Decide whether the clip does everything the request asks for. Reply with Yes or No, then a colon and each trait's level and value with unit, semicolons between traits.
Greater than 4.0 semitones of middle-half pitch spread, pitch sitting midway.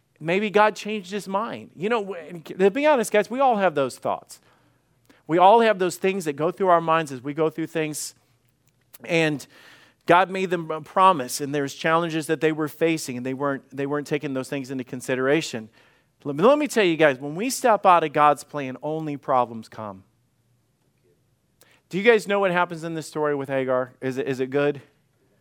Yes: average, 5.2 semitones; medium, 155 Hz